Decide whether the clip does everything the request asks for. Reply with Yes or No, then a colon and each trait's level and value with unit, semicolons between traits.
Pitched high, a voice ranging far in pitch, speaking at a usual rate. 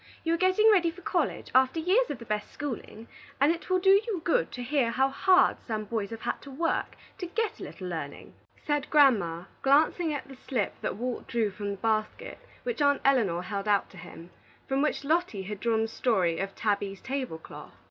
No: very high, 260 Hz; wide, 7.5 semitones; fast, 215 wpm